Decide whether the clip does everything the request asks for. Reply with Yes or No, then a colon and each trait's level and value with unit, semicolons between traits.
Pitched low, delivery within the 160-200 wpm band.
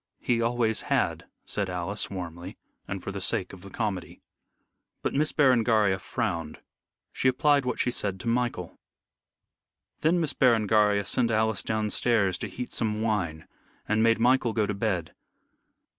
No: low, 110 Hz; average, 150 wpm